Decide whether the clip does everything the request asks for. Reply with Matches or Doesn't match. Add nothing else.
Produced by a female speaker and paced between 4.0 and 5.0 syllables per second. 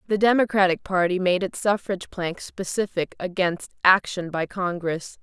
Matches